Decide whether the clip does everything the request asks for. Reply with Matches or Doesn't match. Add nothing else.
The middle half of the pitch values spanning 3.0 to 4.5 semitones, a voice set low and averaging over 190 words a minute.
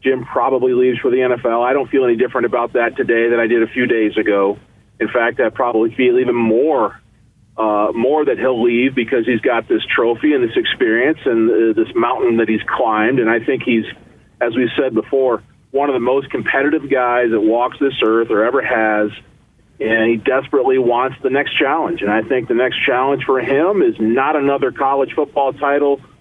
Matches